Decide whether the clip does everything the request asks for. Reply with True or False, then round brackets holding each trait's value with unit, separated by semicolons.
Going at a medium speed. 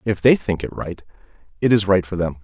False (245 wpm)